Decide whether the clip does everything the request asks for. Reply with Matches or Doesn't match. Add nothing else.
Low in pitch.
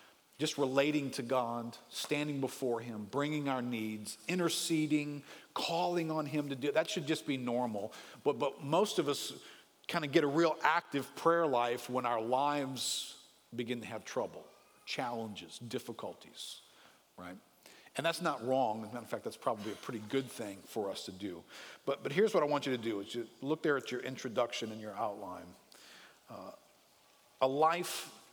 Matches